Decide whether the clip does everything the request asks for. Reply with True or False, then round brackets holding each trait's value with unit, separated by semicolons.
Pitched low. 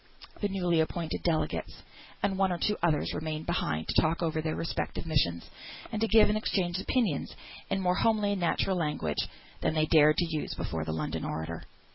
False (165 Hz)